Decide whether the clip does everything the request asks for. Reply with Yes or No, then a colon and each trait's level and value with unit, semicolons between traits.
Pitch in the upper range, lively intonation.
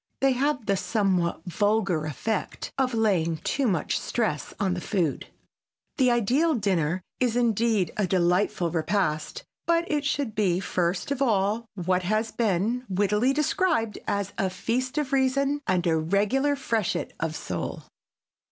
Yes: high, 210 Hz; wide, 5.8 semitones